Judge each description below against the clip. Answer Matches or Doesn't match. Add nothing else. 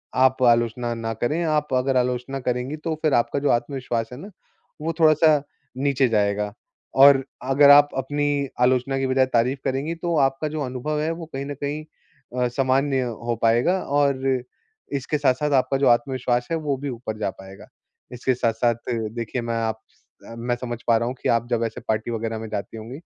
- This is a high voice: Doesn't match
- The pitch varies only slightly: Doesn't match